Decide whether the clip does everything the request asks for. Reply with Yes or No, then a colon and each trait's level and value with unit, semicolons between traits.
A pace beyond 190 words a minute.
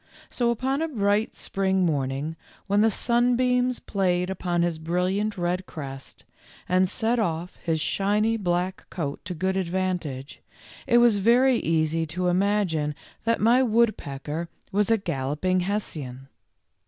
No: slow, 135 wpm